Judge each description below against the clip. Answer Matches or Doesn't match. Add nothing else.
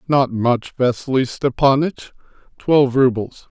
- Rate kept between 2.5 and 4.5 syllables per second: Matches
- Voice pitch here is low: Matches